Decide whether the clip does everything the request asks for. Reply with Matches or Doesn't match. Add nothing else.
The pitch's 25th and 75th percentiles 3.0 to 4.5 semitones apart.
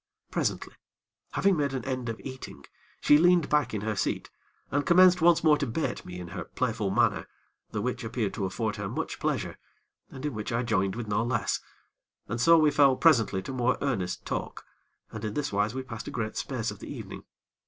Doesn't match